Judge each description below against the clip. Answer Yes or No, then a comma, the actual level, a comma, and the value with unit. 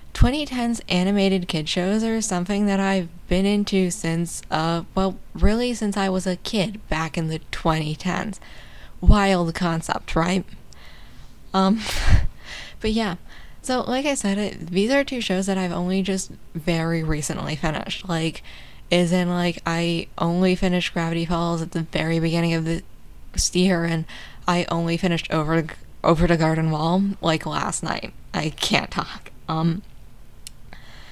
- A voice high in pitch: No, medium, 175 Hz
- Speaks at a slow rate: No, average, 150 wpm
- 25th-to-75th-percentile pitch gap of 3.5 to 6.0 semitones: No, average, 2.8 semitones